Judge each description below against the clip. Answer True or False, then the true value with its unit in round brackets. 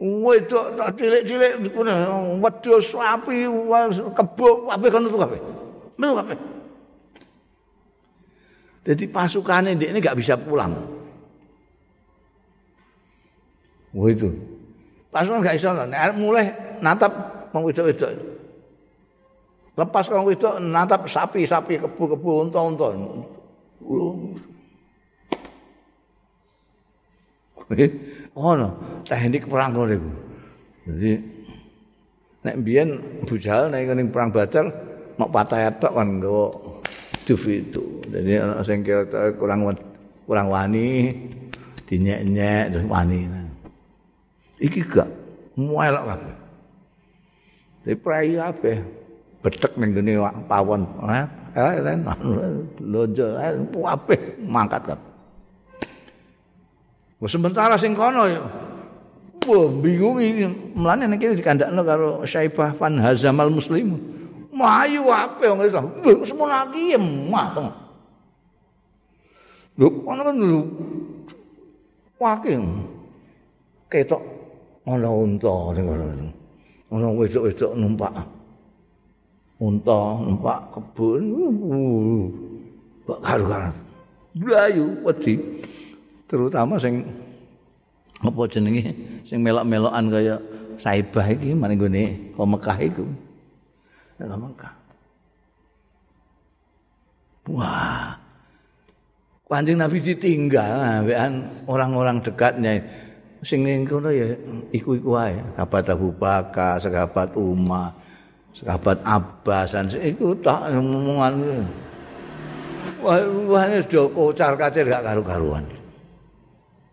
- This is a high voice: False (130 Hz)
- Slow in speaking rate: True (75 wpm)